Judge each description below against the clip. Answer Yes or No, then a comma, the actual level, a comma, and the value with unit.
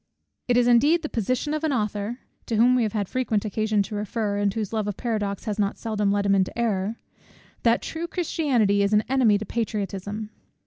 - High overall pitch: Yes, high, 215 Hz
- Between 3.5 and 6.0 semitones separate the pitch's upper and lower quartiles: No, average, 3.1 semitones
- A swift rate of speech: Yes, fast, 210 wpm